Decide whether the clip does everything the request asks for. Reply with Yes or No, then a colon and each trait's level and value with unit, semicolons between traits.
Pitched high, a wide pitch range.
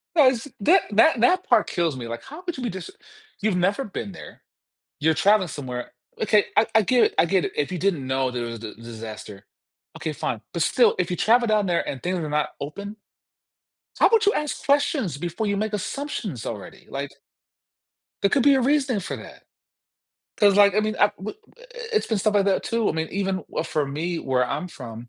Yes: high, 195 Hz; wide, 7.4 semitones